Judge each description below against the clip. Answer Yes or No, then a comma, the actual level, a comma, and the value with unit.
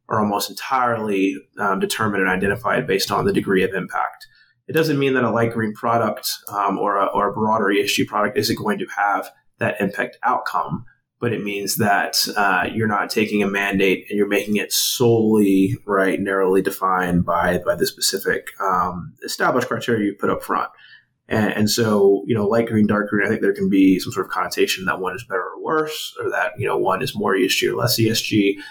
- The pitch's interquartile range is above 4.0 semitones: No, average, 3.1 semitones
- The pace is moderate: No, fast, 210 wpm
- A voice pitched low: Yes, low, 105 Hz